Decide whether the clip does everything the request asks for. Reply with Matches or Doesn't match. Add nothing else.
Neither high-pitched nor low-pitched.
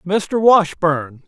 Matches